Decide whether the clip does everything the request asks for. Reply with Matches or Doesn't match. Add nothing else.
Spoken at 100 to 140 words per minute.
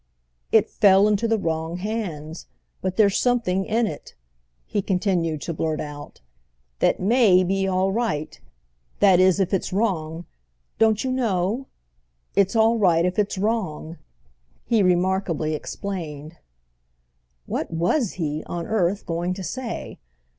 Matches